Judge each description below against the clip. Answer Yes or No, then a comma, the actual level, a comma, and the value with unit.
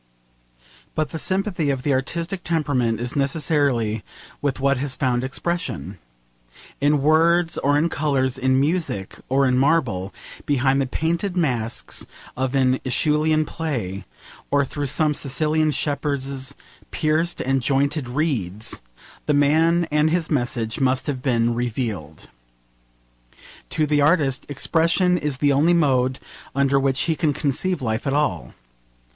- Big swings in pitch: No, average, 3.3 semitones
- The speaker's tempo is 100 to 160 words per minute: Yes, slow, 135 wpm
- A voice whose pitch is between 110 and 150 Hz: Yes, medium, 140 Hz